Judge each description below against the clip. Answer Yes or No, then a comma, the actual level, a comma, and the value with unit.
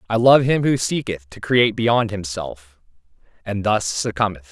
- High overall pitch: No, low, 105 Hz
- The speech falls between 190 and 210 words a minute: No, average, 160 wpm